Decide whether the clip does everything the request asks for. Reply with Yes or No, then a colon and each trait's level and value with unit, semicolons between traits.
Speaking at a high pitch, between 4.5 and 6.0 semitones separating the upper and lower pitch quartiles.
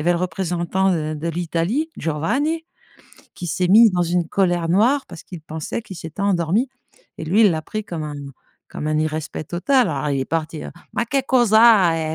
No: medium, 175 Hz; average, 5.1 semitones